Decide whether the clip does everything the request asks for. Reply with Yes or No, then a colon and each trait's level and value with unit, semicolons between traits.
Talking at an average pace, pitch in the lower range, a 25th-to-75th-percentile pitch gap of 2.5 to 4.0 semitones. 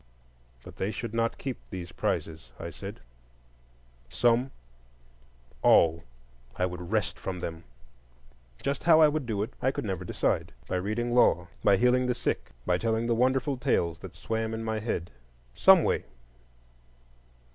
No: average, 150 wpm; low, 110 Hz; wide, 5.6 semitones